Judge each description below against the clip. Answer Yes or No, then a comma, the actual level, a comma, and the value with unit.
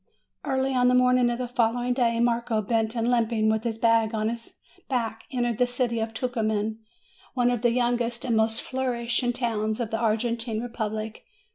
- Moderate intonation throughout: No, narrow, 1.7 semitones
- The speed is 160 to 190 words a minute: Yes, average, 180 wpm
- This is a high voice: Yes, high, 235 Hz